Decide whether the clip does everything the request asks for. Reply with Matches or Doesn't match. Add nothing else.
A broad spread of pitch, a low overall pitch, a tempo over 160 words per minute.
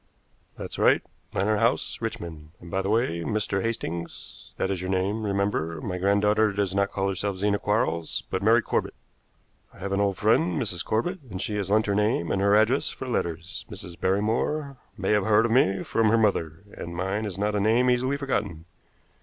Doesn't match